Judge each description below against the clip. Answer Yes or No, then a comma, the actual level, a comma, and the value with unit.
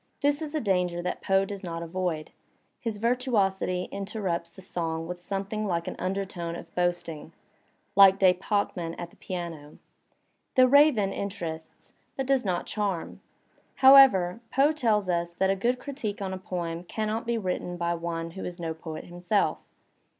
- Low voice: No, high, 190 Hz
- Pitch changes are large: No, average, 3.7 semitones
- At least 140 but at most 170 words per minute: Yes, average, 165 wpm